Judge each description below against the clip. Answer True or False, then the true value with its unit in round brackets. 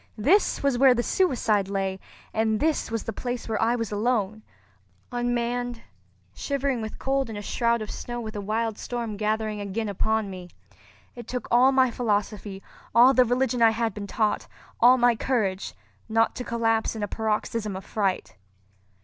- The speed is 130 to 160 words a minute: False (170 wpm)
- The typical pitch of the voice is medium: False (225 Hz)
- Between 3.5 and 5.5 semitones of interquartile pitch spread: False (2.7 semitones)